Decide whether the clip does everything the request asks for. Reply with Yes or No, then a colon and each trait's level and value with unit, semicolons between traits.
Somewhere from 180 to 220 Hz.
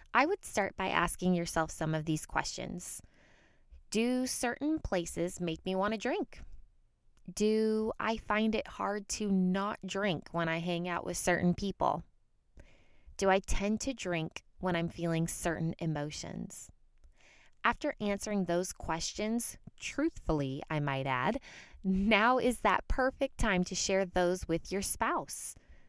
Yes: high, 190 Hz